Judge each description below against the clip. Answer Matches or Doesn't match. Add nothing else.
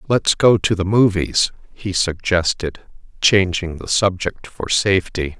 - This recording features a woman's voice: Doesn't match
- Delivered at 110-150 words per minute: Matches